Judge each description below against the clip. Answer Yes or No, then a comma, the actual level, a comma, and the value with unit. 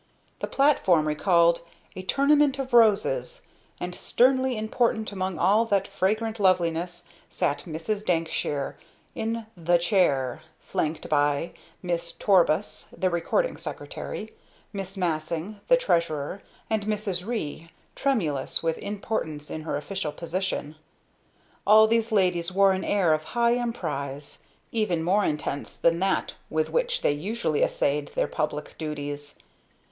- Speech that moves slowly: Yes, slow, 130 wpm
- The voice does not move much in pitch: No, wide, 5.6 semitones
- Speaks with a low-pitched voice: No, medium, 185 Hz